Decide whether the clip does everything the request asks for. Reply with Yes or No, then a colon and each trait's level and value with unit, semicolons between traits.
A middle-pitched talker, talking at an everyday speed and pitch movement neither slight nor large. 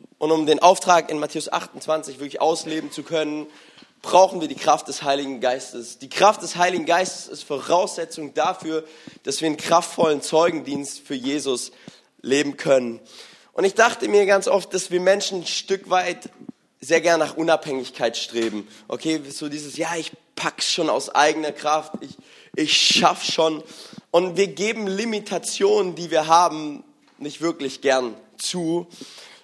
Yes: medium, 160 Hz; average, 155 wpm; average, 3.6 semitones